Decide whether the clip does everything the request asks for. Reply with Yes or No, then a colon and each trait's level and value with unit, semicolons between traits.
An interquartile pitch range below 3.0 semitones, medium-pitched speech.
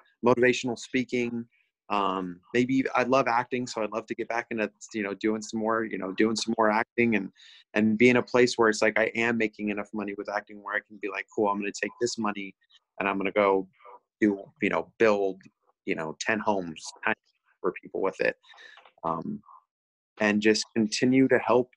No: narrow, 2.6 semitones; low, 110 Hz